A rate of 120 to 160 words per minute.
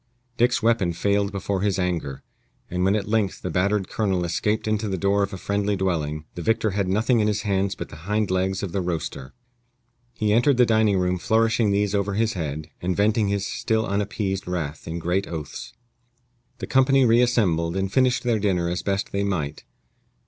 No: average, 195 wpm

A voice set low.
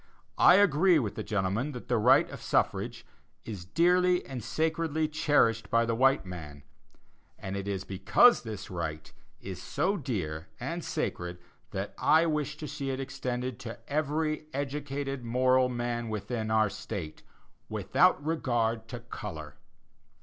Yes: low, 125 Hz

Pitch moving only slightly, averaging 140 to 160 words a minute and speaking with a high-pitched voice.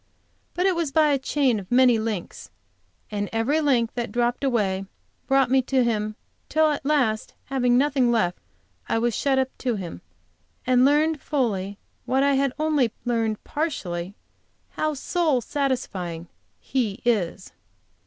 No: average, 4.5 semitones; average, 150 wpm; very high, 250 Hz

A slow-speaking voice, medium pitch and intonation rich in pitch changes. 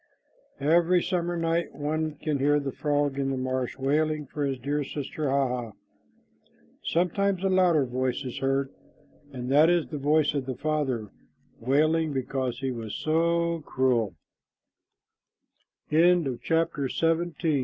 No: slow, 130 wpm; medium, 145 Hz; average, 3.2 semitones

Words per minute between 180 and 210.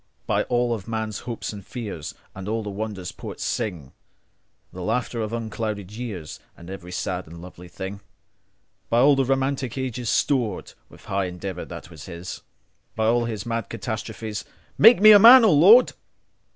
No: average, 145 wpm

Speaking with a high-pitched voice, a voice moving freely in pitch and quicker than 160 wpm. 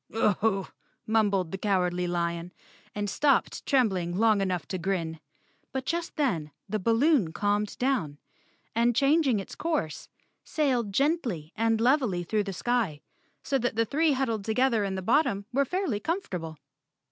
No: high, 215 Hz; wide, 6.3 semitones; average, 150 wpm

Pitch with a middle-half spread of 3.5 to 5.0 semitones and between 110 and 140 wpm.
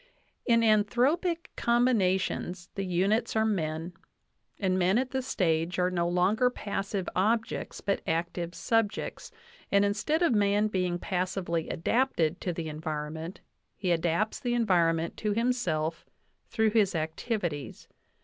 Yes: average, 4.5 semitones; slow, 135 wpm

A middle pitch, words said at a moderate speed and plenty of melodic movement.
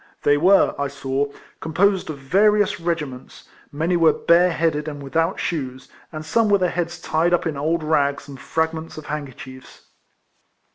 No: medium, 160 Hz; average, 160 wpm; average, 3.4 semitones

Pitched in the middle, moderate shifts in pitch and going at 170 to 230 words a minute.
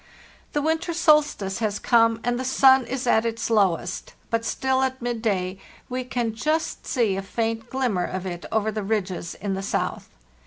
No: high, 230 Hz; average, 4.5 semitones; average, 185 wpm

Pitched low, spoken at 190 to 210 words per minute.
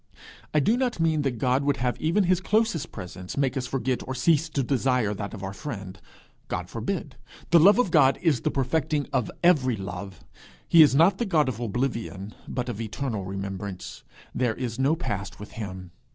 Yes: low, 130 Hz; average, 195 wpm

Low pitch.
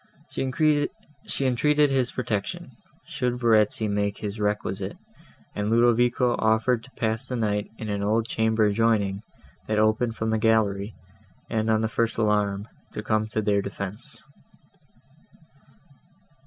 Yes: low, 110 Hz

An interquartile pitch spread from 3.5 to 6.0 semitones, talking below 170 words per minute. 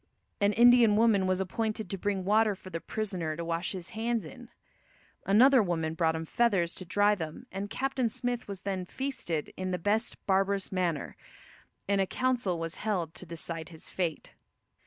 No: average, 4.3 semitones; average, 180 wpm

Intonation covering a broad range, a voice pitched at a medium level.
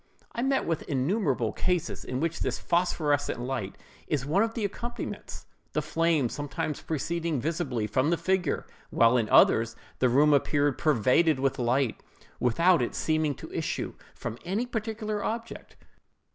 Yes: wide, 5.7 semitones; medium, 150 Hz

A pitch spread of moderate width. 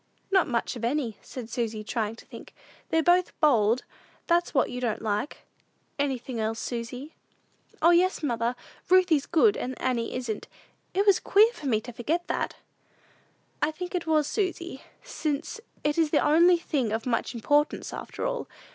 No: wide, 6.6 semitones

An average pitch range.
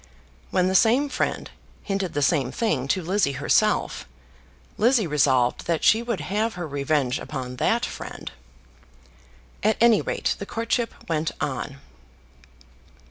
No: wide, 7.8 semitones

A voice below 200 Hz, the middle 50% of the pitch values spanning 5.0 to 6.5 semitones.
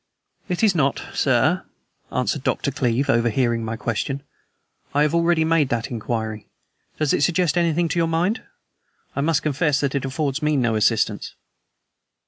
Yes: medium, 140 Hz; wide, 5.6 semitones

